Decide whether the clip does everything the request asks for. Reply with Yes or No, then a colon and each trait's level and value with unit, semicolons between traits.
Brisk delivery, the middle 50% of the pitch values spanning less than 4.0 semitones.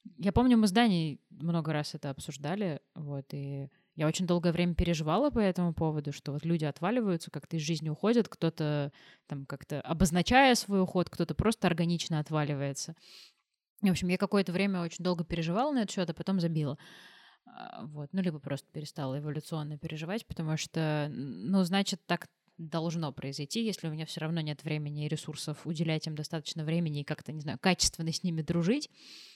Yes: fast, 175 wpm; average, 3.4 semitones